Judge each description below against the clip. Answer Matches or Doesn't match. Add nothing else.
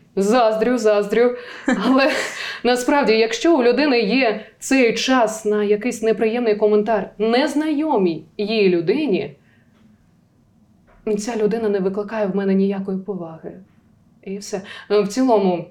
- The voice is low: Doesn't match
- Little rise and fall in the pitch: Doesn't match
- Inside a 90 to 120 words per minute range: Matches